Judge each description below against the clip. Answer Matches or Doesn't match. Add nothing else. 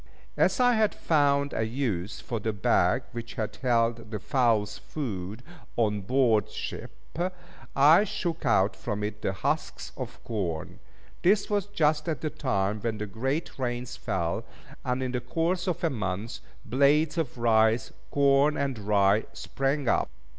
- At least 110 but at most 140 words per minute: Doesn't match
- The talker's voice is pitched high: Doesn't match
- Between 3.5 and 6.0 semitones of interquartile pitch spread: Matches